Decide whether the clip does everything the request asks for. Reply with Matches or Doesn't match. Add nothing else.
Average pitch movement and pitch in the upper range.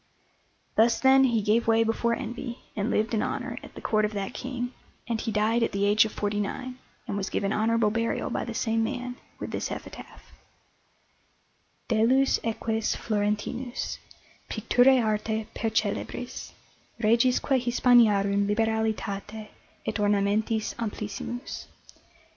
Doesn't match